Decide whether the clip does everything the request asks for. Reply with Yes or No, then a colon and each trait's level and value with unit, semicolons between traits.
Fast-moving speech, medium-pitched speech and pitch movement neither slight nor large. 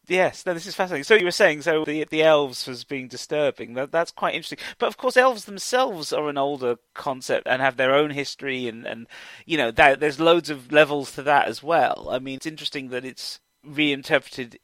Yes: fast, 220 wpm; medium, 150 Hz; average, 3.8 semitones